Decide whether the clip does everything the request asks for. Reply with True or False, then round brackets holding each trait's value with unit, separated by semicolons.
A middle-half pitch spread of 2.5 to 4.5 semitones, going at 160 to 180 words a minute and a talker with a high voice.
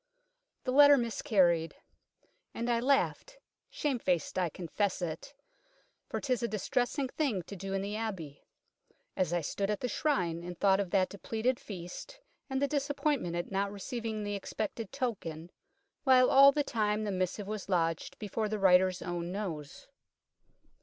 False (5.5 semitones; 165 wpm; 205 Hz)